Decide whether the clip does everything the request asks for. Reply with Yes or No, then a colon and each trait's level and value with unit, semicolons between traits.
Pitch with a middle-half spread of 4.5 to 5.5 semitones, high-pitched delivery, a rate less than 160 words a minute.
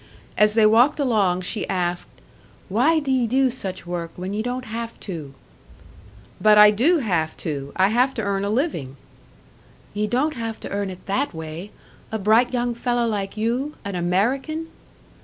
No: average, 4.9 semitones; high, 215 Hz; average, 175 wpm